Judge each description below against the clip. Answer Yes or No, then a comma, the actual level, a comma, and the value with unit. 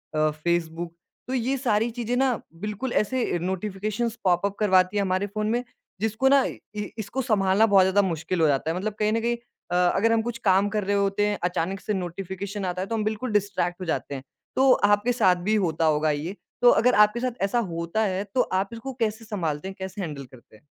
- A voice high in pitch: Yes, high, 200 Hz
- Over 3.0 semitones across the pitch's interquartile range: Yes, average, 3.5 semitones